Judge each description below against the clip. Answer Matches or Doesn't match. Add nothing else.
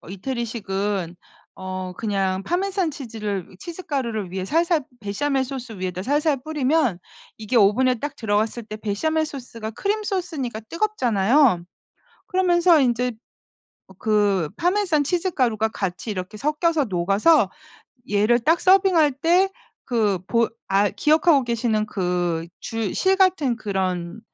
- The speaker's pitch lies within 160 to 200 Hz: Doesn't match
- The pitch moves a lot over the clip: Matches